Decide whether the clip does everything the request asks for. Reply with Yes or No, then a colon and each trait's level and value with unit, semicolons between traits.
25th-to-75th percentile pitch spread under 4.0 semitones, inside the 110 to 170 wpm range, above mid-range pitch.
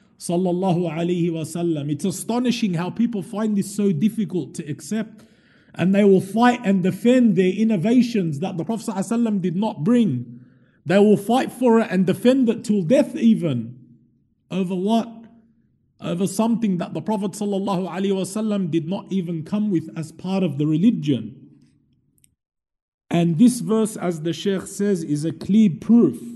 No: average, 4.3 semitones; average, 150 wpm; high, 195 Hz